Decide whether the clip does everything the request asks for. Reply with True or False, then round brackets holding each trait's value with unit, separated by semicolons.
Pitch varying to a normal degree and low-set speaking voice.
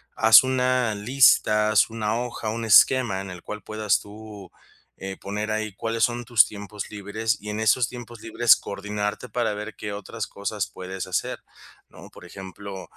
False (2.0 semitones; 105 Hz)